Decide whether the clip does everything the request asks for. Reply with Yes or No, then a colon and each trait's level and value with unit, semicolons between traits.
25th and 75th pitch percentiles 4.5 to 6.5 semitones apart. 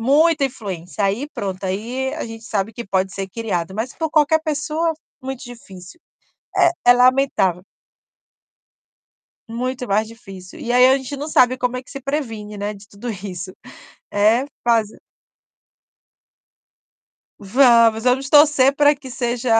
Yes: average, 4.8 semitones